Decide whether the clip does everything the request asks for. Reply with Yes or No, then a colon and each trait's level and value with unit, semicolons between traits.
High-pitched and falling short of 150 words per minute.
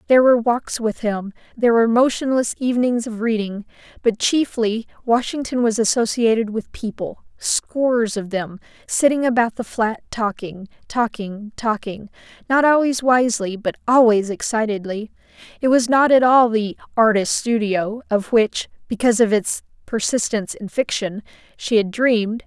Yes: high, 225 Hz; average, 140 wpm